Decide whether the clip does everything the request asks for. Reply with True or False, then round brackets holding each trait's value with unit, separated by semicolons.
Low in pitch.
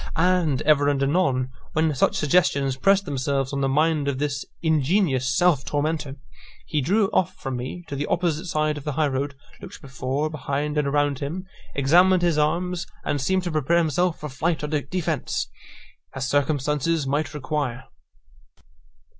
False (150 Hz)